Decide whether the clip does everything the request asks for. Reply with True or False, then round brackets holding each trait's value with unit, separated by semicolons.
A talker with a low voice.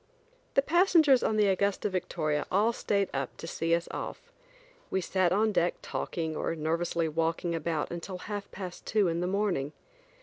False (180 Hz)